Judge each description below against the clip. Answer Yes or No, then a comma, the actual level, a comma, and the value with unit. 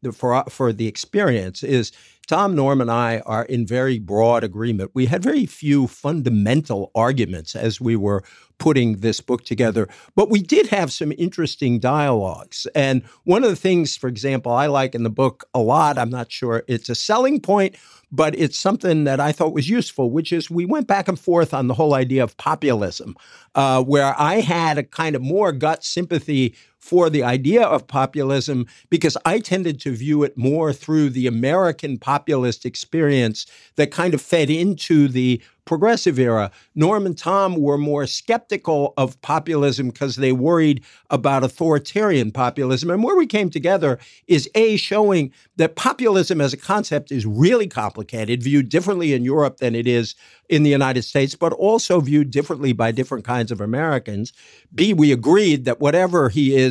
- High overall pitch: No, medium, 140 Hz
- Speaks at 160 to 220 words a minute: Yes, average, 180 wpm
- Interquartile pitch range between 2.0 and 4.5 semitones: No, average, 5.1 semitones